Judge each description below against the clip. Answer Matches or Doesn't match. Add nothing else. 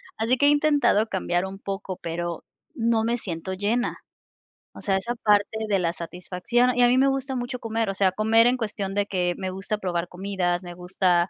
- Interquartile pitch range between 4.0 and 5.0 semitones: Matches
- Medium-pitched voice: Doesn't match